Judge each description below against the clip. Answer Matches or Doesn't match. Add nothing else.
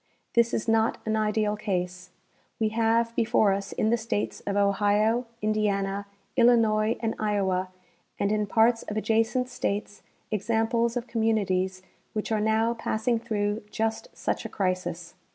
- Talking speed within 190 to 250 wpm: Doesn't match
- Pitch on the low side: Doesn't match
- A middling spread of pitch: Doesn't match